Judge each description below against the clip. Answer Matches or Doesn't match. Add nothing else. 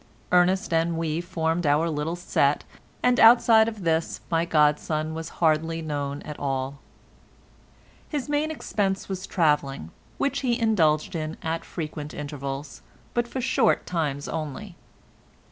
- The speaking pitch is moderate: Matches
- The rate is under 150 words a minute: Matches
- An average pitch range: Matches